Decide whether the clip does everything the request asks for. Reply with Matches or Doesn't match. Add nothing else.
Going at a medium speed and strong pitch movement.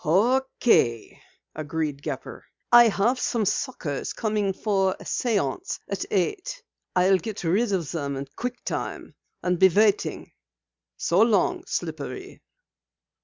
Doesn't match